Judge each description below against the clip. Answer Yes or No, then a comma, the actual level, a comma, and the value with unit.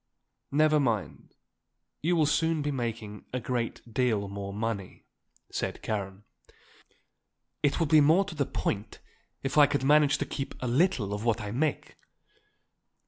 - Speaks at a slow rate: No, average, 150 wpm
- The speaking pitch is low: Yes, low, 130 Hz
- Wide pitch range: Yes, wide, 5.9 semitones